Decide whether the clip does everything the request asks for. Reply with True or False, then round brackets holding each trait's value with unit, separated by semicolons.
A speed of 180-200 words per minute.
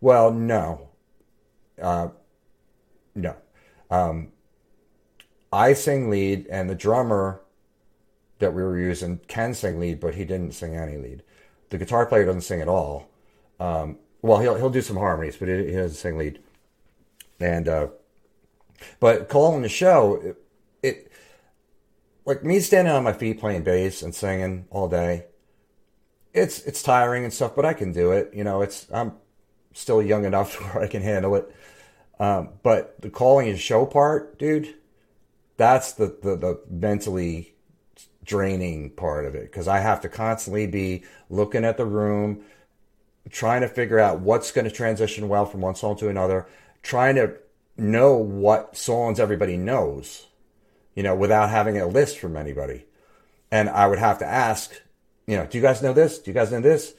False (165 wpm)